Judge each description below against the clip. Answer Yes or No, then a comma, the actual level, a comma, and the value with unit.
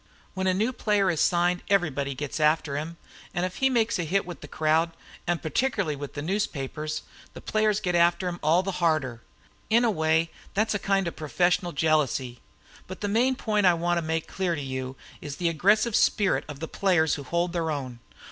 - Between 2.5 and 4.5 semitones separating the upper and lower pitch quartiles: Yes, average, 4.1 semitones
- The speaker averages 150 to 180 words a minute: No, fast, 205 wpm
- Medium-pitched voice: Yes, medium, 170 Hz